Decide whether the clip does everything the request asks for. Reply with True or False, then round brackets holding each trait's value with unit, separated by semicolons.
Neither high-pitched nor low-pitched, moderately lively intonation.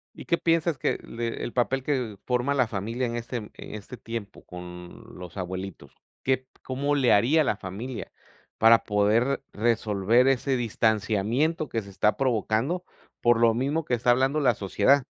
False (120 Hz; 4.0 semitones)